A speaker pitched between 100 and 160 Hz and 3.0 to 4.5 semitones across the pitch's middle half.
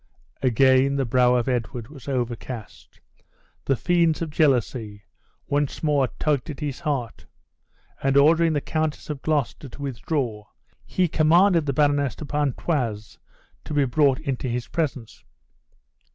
Yes: medium, 140 Hz; average, 3.5 semitones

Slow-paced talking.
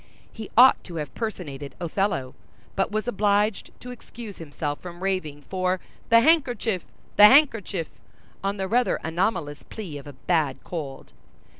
No: average, 145 wpm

